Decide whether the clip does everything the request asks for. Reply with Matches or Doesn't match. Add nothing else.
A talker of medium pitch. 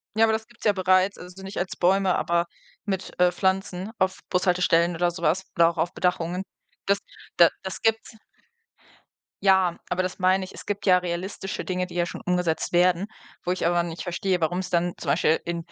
Matches